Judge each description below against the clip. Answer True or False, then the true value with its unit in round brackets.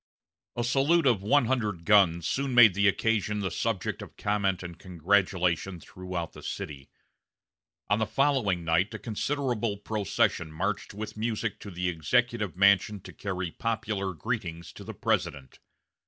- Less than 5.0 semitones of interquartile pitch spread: True (4.0 semitones)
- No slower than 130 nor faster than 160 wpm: True (150 wpm)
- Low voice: True (100 Hz)